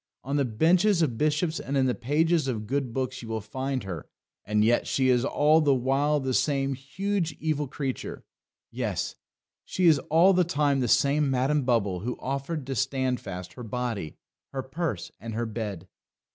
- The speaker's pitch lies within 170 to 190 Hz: No, low, 135 Hz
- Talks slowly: No, average, 180 wpm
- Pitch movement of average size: Yes, average, 3.8 semitones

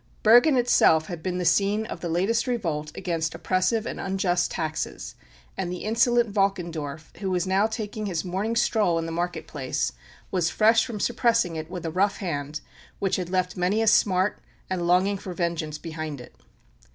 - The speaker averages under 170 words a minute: No, average, 180 wpm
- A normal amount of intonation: Yes, average, 4.1 semitones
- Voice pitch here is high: No, medium, 180 Hz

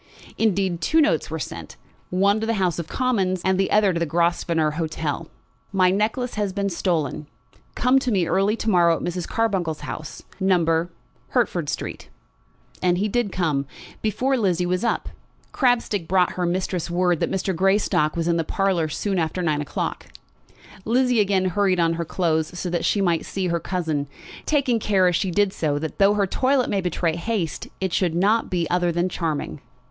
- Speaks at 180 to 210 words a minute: Yes, average, 185 wpm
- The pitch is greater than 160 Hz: Yes, medium, 185 Hz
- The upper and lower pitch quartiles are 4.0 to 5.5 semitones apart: No, average, 3.2 semitones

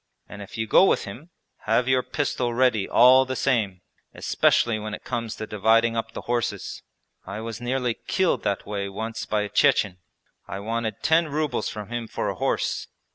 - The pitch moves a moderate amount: Yes, average, 3.1 semitones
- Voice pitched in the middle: No, low, 115 Hz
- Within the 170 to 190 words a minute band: Yes, average, 185 wpm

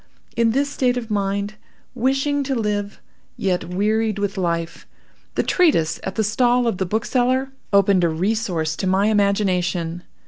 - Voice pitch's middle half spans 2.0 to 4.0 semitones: No, average, 4.4 semitones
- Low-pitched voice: No, high, 205 Hz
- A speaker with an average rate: Yes, average, 150 wpm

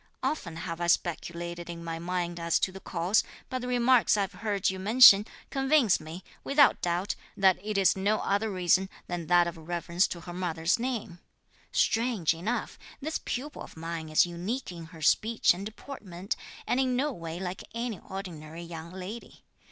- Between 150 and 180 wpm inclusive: Yes, average, 175 wpm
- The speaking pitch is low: No, medium, 185 Hz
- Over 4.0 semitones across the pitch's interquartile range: Yes, average, 4.5 semitones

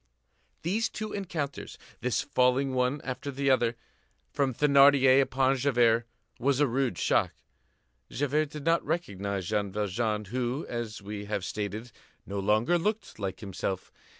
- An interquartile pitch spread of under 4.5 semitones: No, average, 4.9 semitones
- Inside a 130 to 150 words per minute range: Yes, average, 140 wpm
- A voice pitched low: Yes, low, 125 Hz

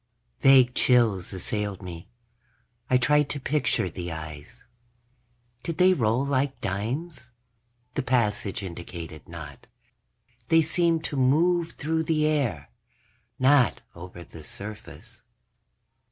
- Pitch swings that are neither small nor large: No, wide, 8.2 semitones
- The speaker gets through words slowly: Yes, slow, 115 wpm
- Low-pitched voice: Yes, low, 125 Hz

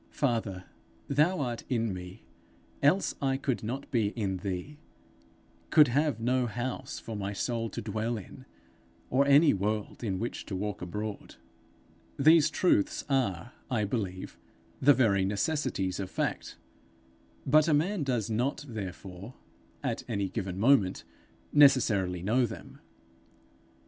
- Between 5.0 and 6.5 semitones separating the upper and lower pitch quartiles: Yes, wide, 5.5 semitones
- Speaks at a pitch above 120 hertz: No, low, 115 Hz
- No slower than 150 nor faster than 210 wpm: No, slow, 135 wpm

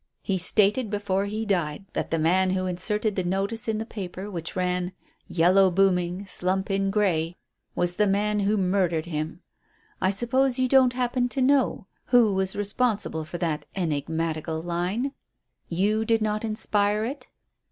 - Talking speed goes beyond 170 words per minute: No, average, 160 wpm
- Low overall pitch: No, high, 195 Hz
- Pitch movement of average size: Yes, average, 3.4 semitones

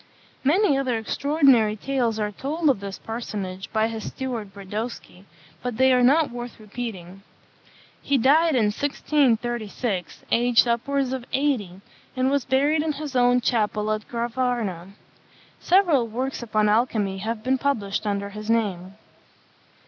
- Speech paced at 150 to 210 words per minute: No, average, 140 wpm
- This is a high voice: Yes, high, 235 Hz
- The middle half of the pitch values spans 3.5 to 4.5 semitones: Yes, average, 4.1 semitones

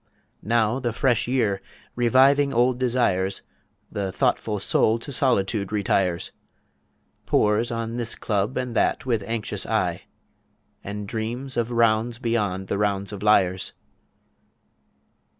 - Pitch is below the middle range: Yes, low, 115 Hz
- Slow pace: Yes, slow, 120 wpm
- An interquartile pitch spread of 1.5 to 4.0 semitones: Yes, average, 3.1 semitones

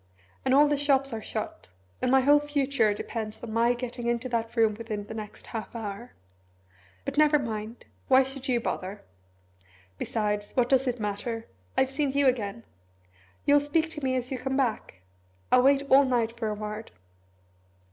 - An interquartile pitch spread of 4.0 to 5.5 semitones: No, average, 3.6 semitones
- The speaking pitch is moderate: No, high, 245 Hz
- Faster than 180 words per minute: No, average, 175 wpm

